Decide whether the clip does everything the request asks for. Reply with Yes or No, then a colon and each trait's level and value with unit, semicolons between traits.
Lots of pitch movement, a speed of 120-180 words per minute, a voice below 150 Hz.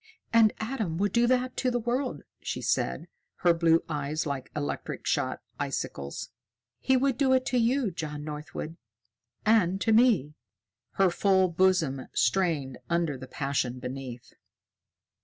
No: wide, 8.0 semitones; average, 140 wpm; medium, 175 Hz